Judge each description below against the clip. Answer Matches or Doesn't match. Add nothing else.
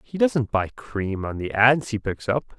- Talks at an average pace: Doesn't match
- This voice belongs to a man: Matches